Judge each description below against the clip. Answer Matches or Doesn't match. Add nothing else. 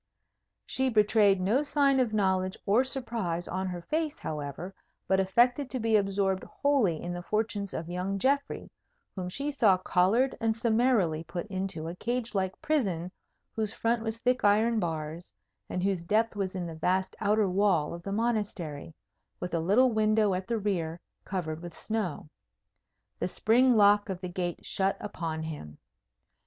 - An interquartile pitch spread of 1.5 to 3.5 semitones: Doesn't match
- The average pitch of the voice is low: Doesn't match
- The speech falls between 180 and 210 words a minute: Doesn't match